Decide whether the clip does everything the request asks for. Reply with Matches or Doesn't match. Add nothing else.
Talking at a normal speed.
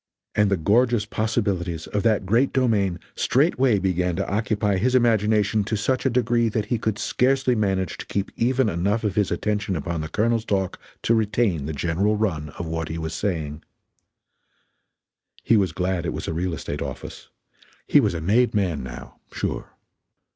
Matches